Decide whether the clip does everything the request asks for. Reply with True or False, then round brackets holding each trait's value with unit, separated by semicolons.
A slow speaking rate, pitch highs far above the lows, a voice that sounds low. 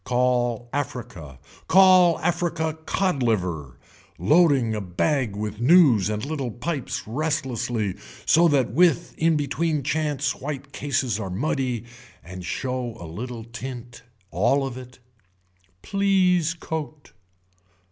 True (115 wpm; 5.7 semitones; 130 Hz)